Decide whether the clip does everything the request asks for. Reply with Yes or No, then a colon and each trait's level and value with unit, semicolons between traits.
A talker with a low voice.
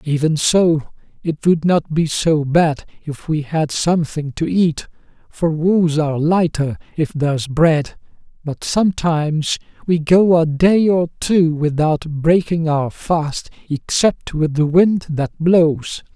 No: medium, 160 Hz